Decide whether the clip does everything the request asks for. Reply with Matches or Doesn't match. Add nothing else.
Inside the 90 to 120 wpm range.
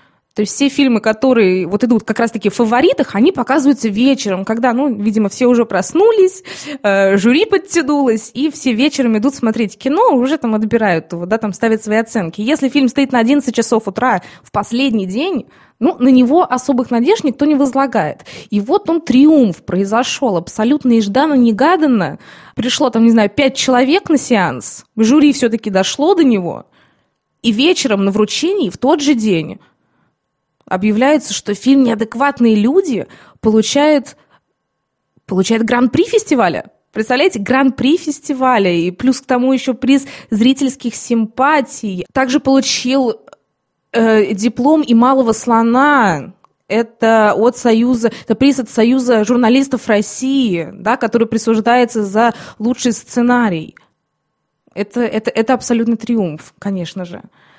Doesn't match